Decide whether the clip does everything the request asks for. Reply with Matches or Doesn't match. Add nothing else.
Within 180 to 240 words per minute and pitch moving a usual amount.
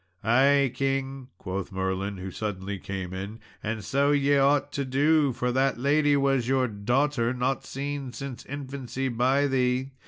Doesn't match